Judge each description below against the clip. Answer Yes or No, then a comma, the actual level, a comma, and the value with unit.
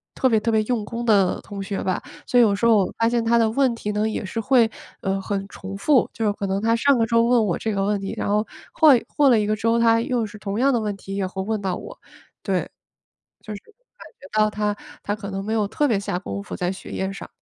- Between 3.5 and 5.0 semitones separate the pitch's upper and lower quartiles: No, average, 2.8 semitones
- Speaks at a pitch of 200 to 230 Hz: Yes, high, 215 Hz